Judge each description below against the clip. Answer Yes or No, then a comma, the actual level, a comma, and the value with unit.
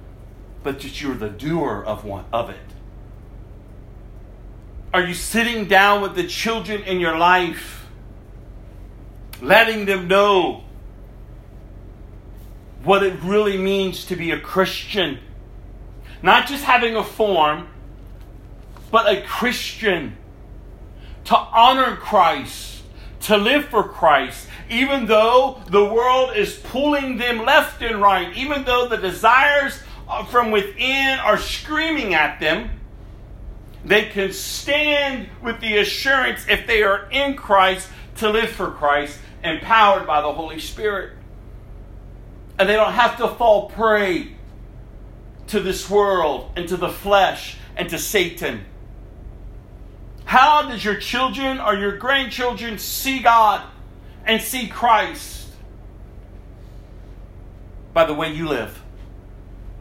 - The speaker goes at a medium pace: No, slow, 120 wpm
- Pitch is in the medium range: Yes, medium, 175 Hz